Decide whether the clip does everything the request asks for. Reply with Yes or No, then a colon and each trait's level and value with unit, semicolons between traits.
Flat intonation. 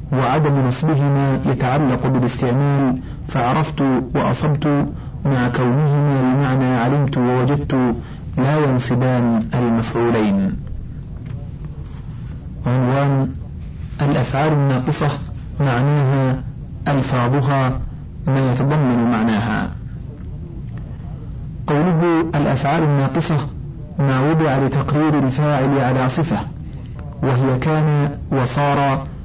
Yes: narrow, 2.3 semitones